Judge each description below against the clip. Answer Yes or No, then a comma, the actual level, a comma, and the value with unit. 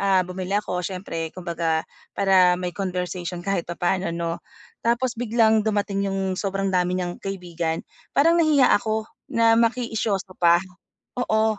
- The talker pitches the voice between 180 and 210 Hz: Yes, high, 190 Hz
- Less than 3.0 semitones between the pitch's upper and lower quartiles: No, average, 3.5 semitones